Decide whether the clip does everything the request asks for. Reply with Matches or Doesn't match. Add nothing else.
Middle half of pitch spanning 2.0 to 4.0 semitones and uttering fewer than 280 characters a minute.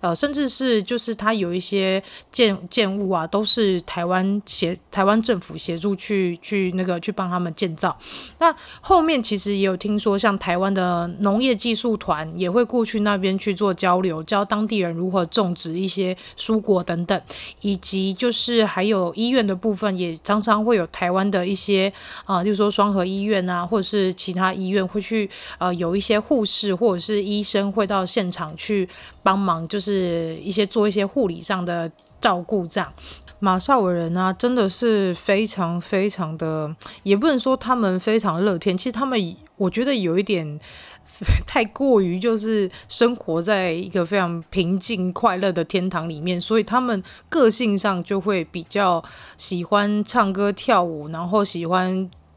Matches